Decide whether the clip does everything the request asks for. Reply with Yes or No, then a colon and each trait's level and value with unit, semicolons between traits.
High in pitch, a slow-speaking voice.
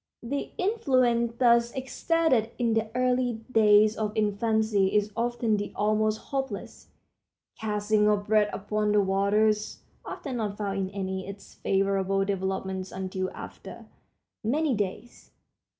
Yes: high, 215 Hz; slow, 125 wpm